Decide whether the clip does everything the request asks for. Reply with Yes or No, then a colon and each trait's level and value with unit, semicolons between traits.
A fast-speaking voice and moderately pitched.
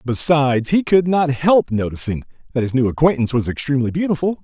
No: average, 175 wpm; medium, 145 Hz